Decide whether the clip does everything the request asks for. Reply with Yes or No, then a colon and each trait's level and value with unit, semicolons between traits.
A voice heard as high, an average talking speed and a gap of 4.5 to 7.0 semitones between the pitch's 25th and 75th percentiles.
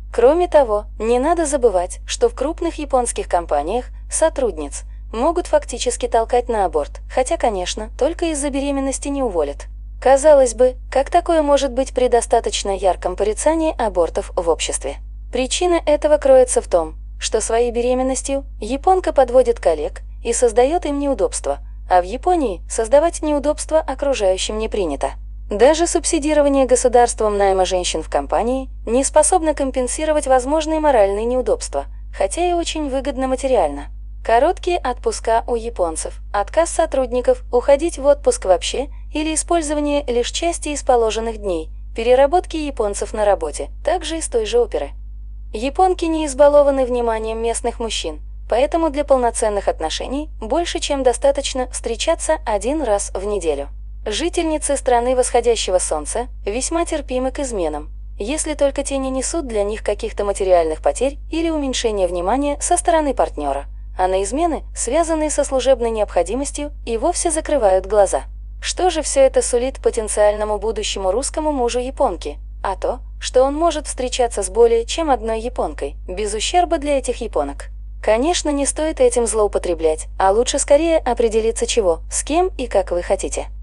Yes: very high, 265 Hz; average, 140 wpm; wide, 5.6 semitones